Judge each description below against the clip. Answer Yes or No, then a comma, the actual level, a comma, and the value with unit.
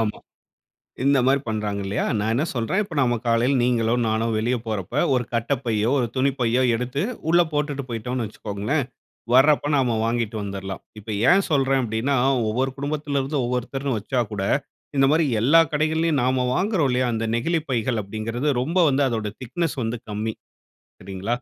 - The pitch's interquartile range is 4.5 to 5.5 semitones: No, average, 3.9 semitones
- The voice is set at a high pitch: No, low, 125 Hz